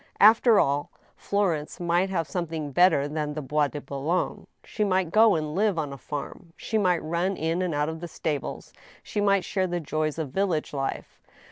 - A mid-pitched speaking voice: Yes, medium, 165 Hz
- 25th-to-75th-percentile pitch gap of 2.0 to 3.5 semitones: No, average, 3.9 semitones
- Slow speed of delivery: No, average, 195 wpm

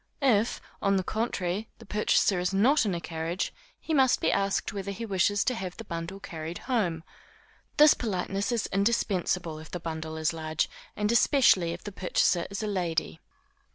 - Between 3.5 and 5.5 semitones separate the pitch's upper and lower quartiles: Yes, average, 4.0 semitones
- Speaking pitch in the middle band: No, high, 195 Hz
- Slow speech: No, average, 180 wpm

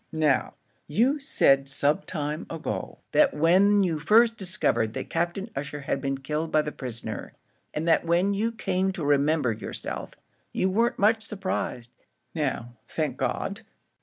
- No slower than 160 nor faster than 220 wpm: No, average, 150 wpm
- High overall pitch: No, medium, 160 Hz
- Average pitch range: No, wide, 5.8 semitones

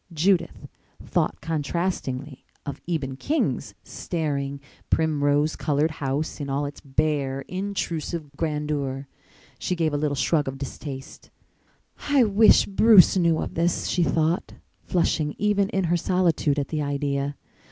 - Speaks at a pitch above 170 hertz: No, medium, 155 Hz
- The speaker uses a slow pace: Yes, slow, 130 wpm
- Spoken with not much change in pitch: No, average, 3.5 semitones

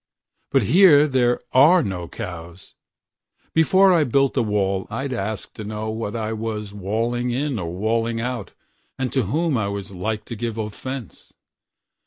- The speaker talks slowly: No, average, 145 wpm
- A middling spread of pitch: Yes, average, 4.3 semitones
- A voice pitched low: Yes, low, 115 Hz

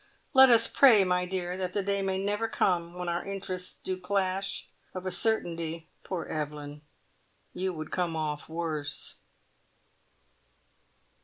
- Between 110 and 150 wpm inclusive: Yes, average, 140 wpm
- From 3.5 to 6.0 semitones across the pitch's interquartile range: No, average, 2.7 semitones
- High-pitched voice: No, medium, 180 Hz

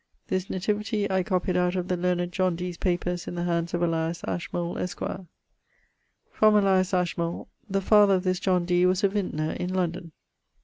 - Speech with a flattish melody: Yes, narrow, 1.4 semitones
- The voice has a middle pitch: Yes, medium, 180 Hz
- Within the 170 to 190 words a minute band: Yes, average, 180 wpm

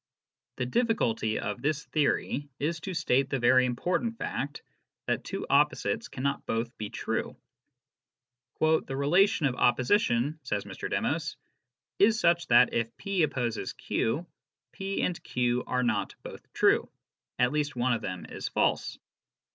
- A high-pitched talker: No, low, 135 Hz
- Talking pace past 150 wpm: No, average, 145 wpm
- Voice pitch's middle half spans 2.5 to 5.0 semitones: No, wide, 5.5 semitones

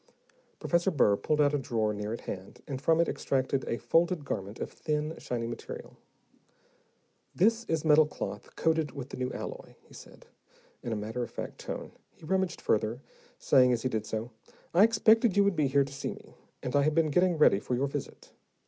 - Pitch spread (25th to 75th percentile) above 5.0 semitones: Yes, wide, 5.5 semitones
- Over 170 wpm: Yes, average, 200 wpm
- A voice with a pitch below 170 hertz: Yes, medium, 140 Hz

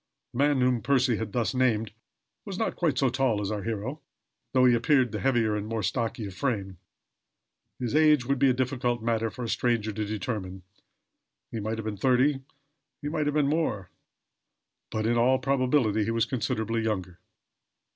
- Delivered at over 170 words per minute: Yes, average, 185 wpm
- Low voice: Yes, low, 120 Hz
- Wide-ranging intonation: No, average, 3.3 semitones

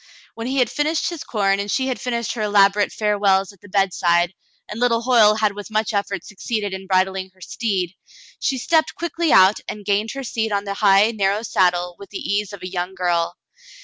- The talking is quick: Yes, fast, 210 wpm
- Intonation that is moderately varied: Yes, average, 3.0 semitones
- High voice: Yes, high, 205 Hz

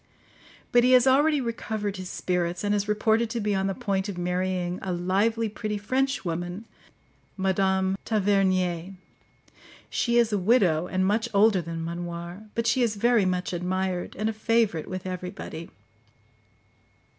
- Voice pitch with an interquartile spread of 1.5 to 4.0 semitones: Yes, average, 3.5 semitones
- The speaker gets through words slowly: No, average, 150 wpm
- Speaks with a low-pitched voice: No, high, 195 Hz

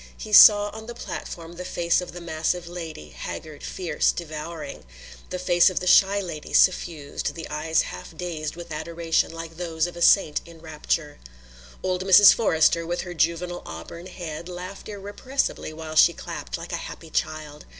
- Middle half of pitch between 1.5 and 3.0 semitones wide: Yes, narrow, 2.4 semitones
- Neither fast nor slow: Yes, average, 170 wpm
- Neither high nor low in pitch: Yes, medium, 170 Hz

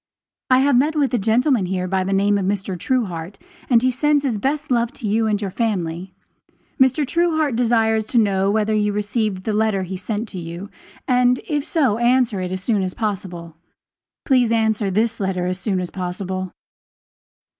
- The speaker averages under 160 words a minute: No, average, 190 wpm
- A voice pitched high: Yes, high, 215 Hz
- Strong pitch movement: No, average, 4.6 semitones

